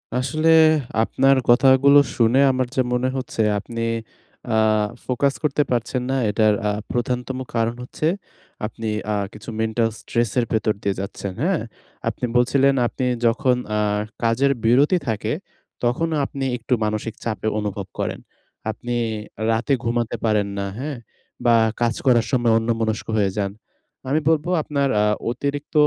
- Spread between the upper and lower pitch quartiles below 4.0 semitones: Yes, average, 3.4 semitones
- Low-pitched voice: Yes, low, 120 Hz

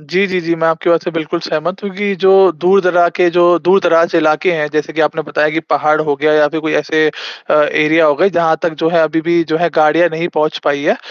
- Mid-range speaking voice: Yes, medium, 160 Hz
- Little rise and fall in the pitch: Yes, narrow, 2.3 semitones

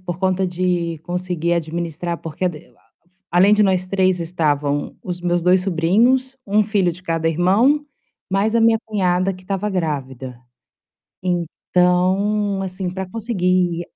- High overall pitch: No, medium, 180 Hz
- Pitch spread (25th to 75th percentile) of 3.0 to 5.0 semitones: No, narrow, 2.4 semitones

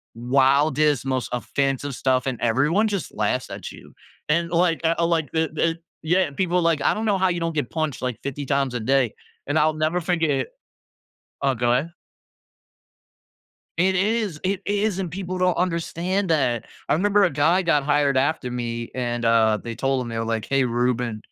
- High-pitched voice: No, medium, 145 Hz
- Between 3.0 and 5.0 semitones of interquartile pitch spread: No, wide, 5.4 semitones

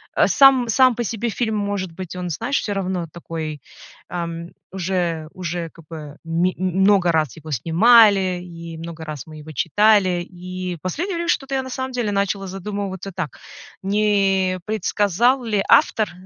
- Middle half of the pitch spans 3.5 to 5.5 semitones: Yes, average, 3.9 semitones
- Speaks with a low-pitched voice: No, medium, 185 Hz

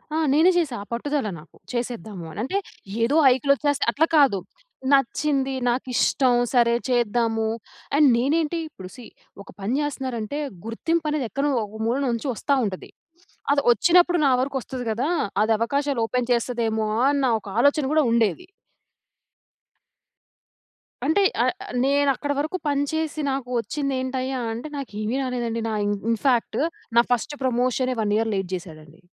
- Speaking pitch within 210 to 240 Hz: No, very high, 255 Hz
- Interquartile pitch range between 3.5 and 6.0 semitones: Yes, average, 3.8 semitones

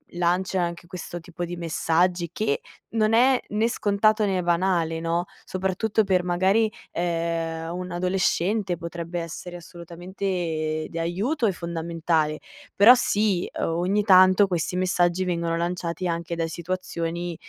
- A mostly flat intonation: Yes, narrow, 2.0 semitones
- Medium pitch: Yes, medium, 175 Hz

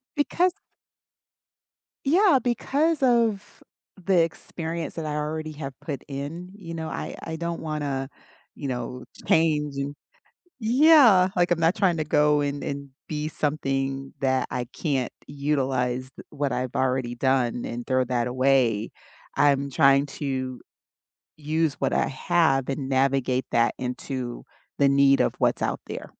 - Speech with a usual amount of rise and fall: Yes, average, 3.9 semitones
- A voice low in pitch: No, medium, 145 Hz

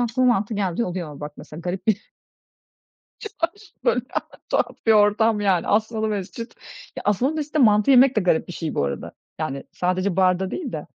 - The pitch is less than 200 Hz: No, high, 205 Hz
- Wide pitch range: No, average, 4.5 semitones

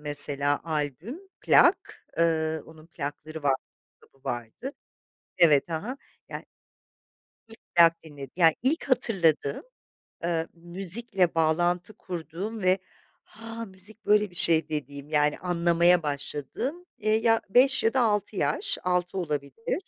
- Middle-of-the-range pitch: Yes, medium, 170 Hz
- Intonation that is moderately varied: No, wide, 5.7 semitones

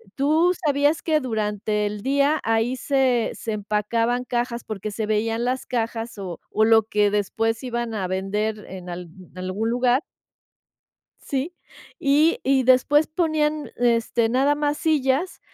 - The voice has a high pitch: Yes, high, 235 Hz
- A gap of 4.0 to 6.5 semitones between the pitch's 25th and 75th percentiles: Yes, average, 4.7 semitones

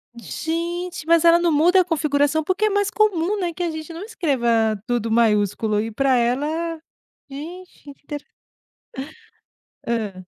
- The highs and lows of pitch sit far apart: Yes, wide, 6.5 semitones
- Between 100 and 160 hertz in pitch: No, very high, 315 Hz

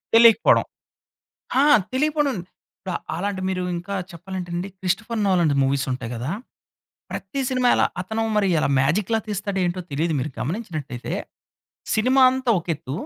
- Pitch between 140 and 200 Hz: Yes, high, 190 Hz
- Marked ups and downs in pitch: Yes, wide, 5.7 semitones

